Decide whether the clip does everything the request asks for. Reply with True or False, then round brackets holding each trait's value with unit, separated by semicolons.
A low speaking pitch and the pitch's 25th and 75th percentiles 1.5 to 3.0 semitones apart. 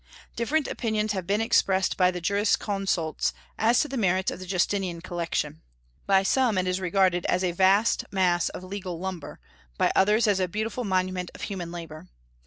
False (190 Hz; 2.5 semitones)